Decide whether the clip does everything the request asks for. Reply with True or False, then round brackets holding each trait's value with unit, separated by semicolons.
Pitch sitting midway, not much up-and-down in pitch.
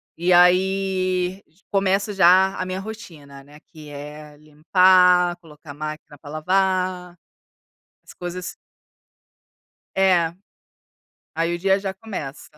False (180 Hz; 3.7 semitones)